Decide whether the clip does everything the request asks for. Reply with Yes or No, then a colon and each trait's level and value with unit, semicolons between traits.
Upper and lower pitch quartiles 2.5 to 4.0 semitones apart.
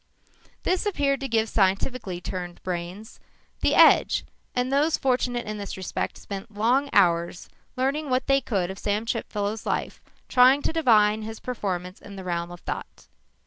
No: average, 5.2 semitones